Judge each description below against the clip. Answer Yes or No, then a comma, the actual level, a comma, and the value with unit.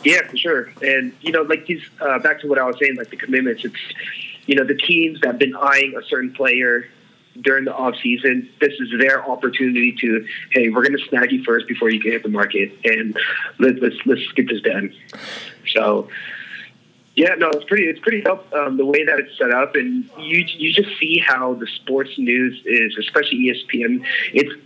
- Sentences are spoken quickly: Yes, fast, 210 wpm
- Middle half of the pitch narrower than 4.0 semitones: No, average, 4.3 semitones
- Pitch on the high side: No, low, 135 Hz